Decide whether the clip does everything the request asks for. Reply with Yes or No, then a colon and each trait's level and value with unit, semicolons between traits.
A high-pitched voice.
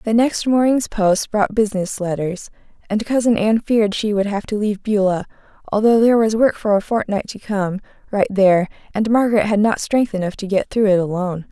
Yes: high, 210 Hz